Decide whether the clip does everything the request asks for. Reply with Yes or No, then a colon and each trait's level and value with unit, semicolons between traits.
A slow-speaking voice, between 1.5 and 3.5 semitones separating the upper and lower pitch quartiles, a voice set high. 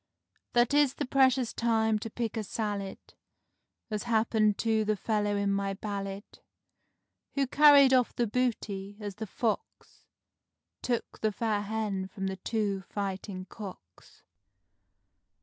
Yes: slow, 130 wpm; average, 2.9 semitones; high, 215 Hz